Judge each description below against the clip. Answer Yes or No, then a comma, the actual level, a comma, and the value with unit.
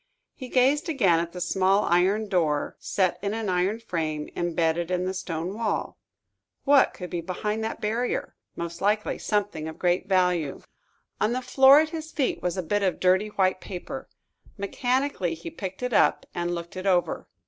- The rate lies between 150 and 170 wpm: No, average, 180 wpm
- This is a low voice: No, high, 190 Hz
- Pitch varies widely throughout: No, average, 4.1 semitones